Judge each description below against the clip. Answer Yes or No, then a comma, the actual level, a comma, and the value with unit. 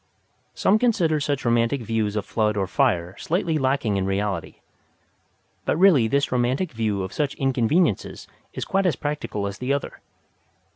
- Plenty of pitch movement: Yes, wide, 6.1 semitones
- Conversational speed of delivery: Yes, average, 155 wpm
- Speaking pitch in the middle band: No, low, 125 Hz